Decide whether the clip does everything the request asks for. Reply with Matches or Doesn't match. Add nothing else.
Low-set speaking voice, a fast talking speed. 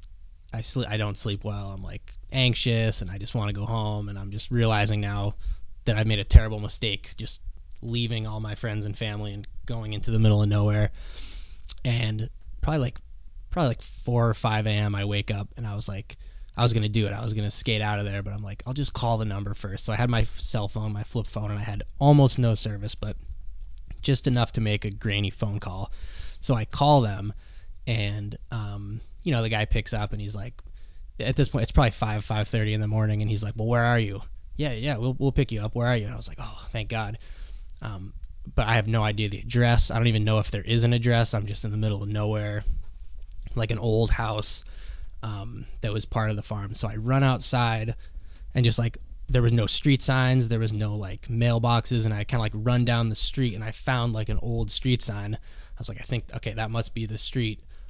Matches